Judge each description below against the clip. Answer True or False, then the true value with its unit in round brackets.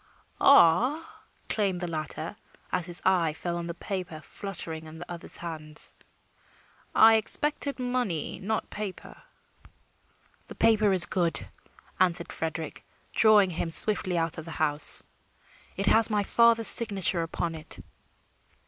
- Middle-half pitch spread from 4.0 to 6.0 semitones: True (4.5 semitones)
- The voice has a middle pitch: True (180 Hz)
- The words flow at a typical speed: False (130 wpm)